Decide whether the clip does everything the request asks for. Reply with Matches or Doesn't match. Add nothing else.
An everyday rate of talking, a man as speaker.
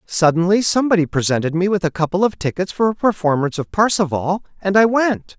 Matches